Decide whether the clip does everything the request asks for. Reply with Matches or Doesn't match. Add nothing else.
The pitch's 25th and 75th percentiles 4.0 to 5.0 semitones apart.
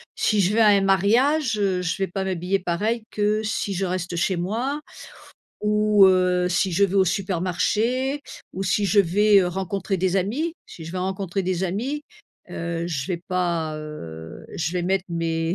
Doesn't match